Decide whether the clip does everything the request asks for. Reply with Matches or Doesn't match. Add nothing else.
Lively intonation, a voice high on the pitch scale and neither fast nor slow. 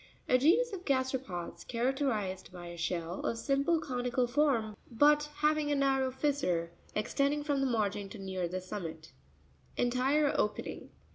Matches